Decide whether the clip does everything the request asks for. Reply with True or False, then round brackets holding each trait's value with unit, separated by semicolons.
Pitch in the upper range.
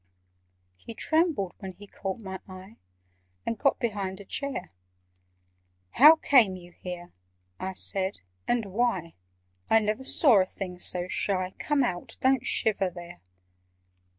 True (195 Hz)